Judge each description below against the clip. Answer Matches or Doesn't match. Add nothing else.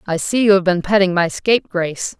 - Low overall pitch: Doesn't match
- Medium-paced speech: Doesn't match